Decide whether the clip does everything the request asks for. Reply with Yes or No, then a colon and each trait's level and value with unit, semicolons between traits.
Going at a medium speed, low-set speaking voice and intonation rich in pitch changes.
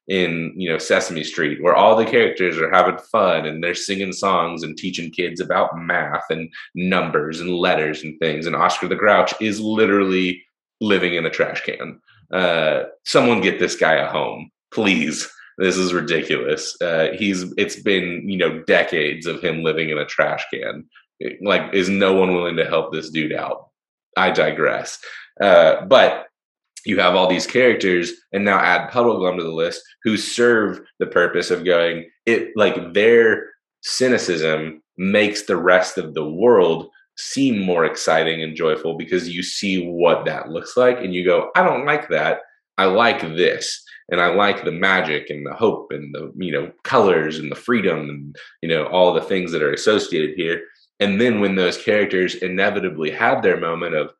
Yes: average, 180 wpm; very low, 95 Hz; wide, 6.7 semitones